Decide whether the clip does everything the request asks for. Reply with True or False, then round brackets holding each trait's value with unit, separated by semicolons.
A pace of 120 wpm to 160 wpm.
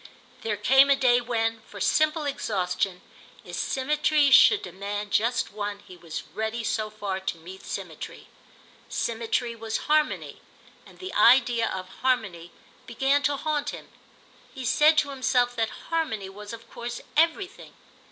True (145 wpm)